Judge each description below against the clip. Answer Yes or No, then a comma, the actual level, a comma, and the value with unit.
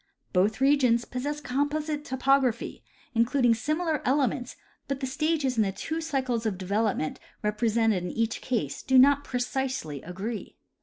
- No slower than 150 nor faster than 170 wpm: No, average, 140 wpm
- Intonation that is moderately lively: Yes, average, 4.1 semitones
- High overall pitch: Yes, very high, 250 Hz